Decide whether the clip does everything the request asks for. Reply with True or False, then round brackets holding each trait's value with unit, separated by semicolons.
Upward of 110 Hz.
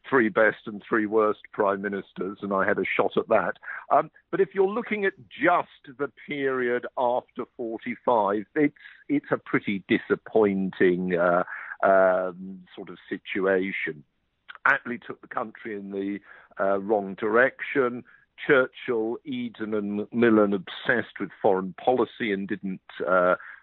False (105 Hz)